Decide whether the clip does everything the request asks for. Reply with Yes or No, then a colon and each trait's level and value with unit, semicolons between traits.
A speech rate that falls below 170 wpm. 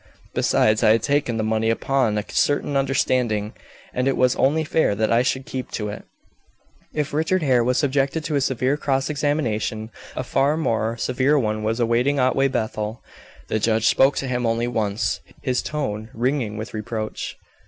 No: average, 175 wpm